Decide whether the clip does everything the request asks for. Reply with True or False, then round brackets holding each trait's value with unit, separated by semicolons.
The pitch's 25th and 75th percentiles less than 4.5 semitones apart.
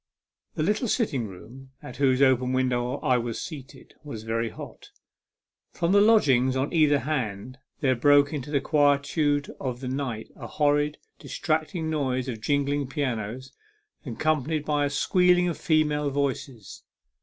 True (2.9 semitones)